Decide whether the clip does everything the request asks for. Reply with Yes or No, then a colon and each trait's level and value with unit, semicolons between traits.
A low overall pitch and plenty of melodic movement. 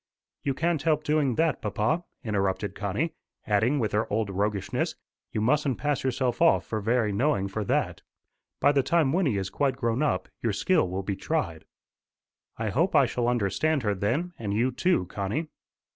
Yes: low, 120 Hz; wide, 6.3 semitones